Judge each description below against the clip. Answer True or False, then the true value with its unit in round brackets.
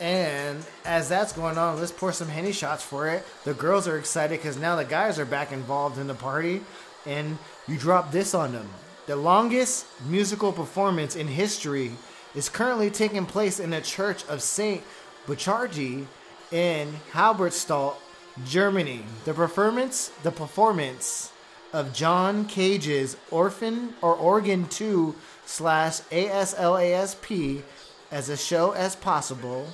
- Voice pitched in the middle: True (170 Hz)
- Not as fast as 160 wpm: True (150 wpm)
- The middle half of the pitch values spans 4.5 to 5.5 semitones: True (4.8 semitones)